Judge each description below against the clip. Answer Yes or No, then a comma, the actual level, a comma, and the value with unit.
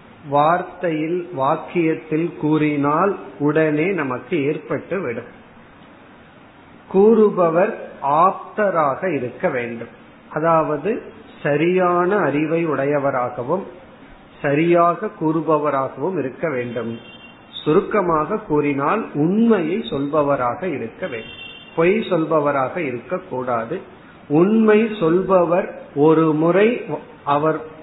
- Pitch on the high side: No, medium, 160 Hz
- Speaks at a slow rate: Yes, slow, 65 wpm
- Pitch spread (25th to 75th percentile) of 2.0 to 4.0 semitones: Yes, average, 3.6 semitones